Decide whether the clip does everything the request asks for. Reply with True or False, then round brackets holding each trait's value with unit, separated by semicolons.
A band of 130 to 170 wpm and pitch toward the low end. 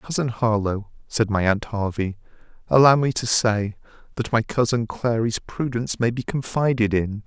True (155 wpm; 115 Hz)